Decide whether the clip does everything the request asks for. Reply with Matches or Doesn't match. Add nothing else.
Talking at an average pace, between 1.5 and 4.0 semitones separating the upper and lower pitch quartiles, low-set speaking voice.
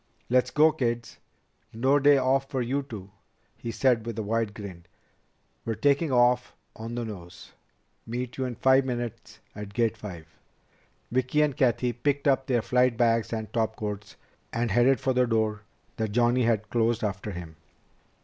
Matches